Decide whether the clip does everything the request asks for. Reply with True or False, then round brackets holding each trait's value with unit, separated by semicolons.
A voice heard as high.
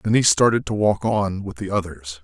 False (100 Hz)